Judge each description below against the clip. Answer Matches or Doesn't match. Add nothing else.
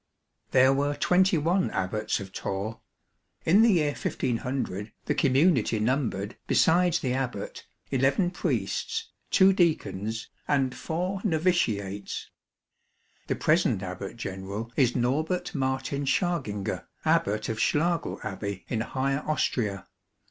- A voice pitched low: Matches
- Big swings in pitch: Matches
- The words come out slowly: Matches